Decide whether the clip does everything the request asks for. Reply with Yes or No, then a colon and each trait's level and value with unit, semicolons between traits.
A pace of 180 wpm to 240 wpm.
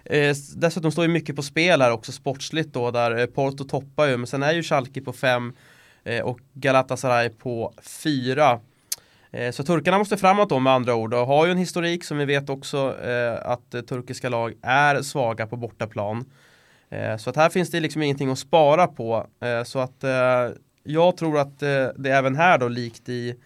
Yes: average, 200 wpm